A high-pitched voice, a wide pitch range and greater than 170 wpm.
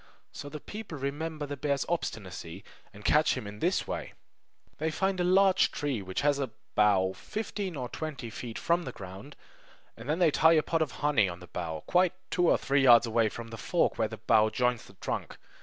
No: medium, 140 Hz; wide, 6.8 semitones; fast, 205 wpm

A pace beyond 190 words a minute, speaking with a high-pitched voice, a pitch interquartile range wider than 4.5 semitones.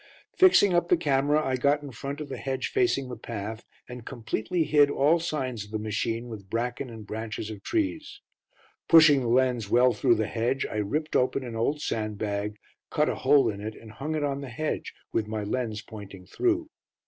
No: average, 200 wpm; low, 125 Hz; average, 5.1 semitones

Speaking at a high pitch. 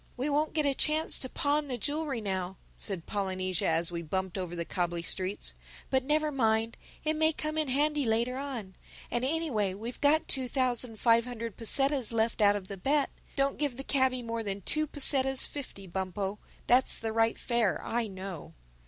Yes: high, 235 Hz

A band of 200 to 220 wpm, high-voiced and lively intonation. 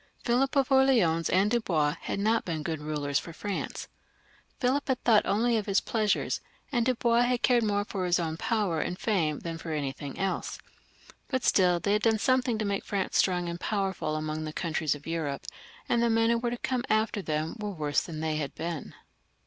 Yes: fast, 205 wpm; high, 195 Hz; wide, 6.4 semitones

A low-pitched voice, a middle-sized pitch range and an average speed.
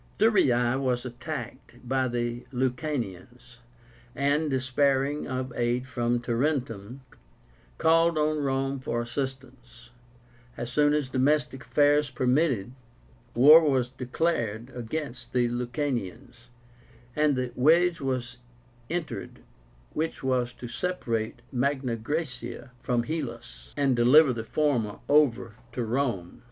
No: low, 130 Hz; average, 3.2 semitones; slow, 110 wpm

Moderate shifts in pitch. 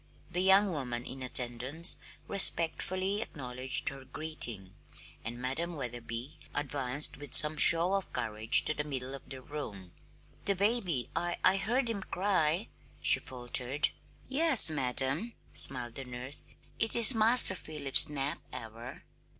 No: wide, 6.8 semitones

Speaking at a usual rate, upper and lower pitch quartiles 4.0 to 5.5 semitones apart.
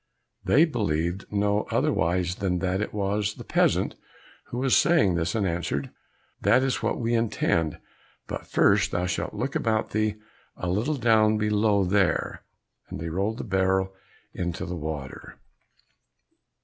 No: average, 150 wpm; average, 3.6 semitones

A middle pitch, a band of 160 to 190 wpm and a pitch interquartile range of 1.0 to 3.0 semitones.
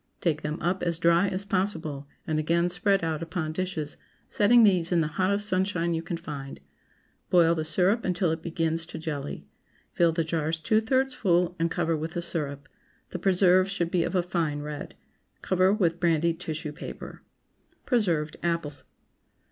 Yes: medium, 170 Hz; average, 170 wpm; narrow, 2.6 semitones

